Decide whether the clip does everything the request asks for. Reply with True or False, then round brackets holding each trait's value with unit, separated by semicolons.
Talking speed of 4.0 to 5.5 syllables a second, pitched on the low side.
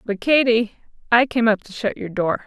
False (4.8 syllables/s; 220 Hz)